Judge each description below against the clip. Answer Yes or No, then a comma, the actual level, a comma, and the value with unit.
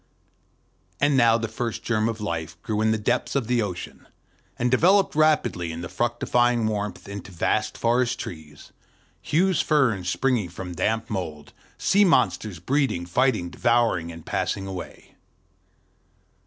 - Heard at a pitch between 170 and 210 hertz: No, low, 110 Hz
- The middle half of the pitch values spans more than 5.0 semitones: Yes, wide, 5.5 semitones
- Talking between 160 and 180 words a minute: No, average, 145 wpm